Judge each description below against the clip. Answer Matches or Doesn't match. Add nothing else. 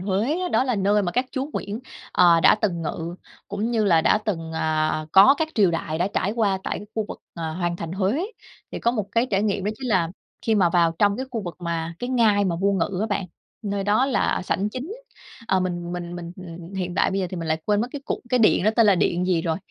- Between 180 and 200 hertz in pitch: Matches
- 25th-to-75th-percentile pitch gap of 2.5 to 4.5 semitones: Matches